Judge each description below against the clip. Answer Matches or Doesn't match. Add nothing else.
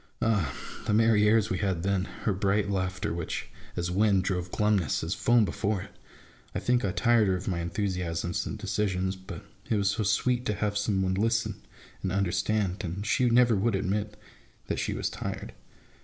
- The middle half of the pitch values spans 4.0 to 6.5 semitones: Doesn't match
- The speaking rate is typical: Matches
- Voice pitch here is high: Doesn't match